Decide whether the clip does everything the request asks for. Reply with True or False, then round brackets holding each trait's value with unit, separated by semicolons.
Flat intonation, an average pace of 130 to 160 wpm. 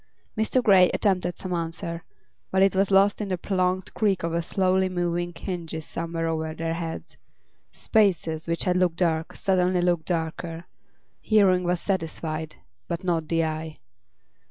True (2.3 semitones; 150 wpm)